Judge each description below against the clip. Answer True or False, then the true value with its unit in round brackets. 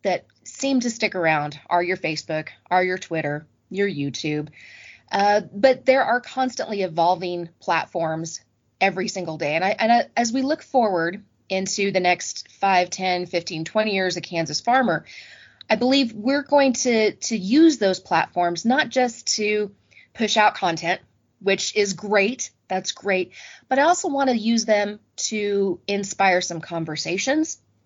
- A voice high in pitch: True (195 Hz)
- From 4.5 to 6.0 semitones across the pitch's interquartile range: True (5.1 semitones)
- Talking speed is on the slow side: False (155 wpm)